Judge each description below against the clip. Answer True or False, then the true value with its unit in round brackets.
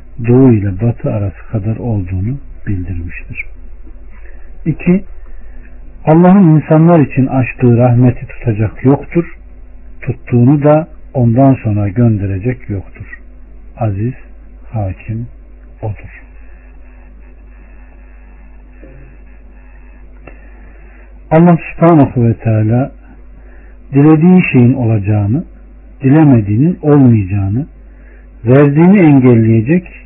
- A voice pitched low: True (120 Hz)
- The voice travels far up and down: True (5.7 semitones)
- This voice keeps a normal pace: False (70 wpm)